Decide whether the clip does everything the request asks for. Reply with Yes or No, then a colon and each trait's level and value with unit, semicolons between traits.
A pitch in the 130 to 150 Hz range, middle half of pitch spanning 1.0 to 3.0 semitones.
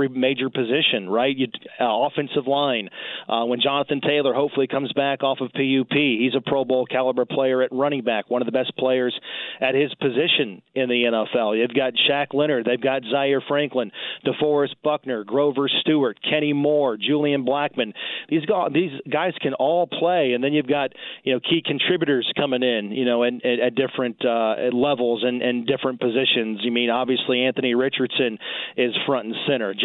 Yes: low, 135 Hz; narrow, 2.4 semitones